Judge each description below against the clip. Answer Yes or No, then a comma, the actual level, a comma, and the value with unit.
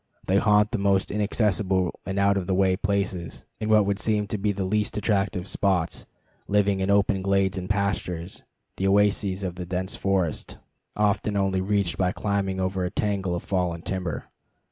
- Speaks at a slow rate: No, average, 190 wpm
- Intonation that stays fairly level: Yes, narrow, 1.6 semitones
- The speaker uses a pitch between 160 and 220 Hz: No, very low, 95 Hz